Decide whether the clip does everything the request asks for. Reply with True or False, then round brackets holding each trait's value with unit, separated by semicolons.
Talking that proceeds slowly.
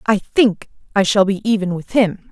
False (205 wpm)